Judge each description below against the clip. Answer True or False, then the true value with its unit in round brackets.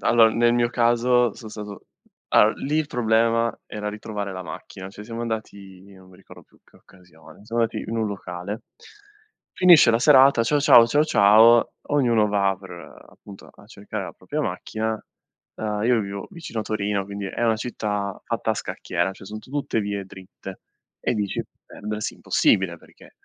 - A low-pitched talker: True (110 Hz)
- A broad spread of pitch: False (2.8 semitones)